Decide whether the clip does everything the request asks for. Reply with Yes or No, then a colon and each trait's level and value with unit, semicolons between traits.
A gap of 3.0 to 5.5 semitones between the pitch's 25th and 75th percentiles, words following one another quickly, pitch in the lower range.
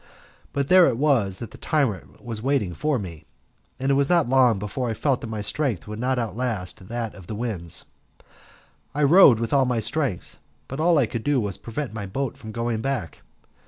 Yes: average, 4.5 semitones; fast, 210 wpm; low, 120 Hz